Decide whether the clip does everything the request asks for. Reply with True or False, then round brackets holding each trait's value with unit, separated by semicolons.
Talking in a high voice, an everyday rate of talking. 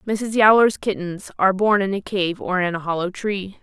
False (195 Hz; 215 wpm)